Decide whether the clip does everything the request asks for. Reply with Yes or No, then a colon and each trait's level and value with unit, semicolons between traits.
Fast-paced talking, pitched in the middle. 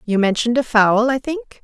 No: fast, 220 wpm; high, 235 Hz